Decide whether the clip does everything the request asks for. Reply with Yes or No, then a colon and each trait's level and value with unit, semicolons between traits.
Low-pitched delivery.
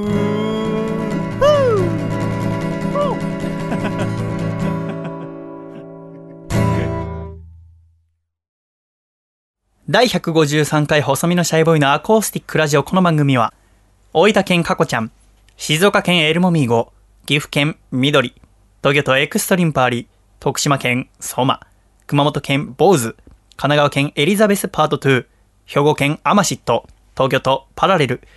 No: medium, 145 Hz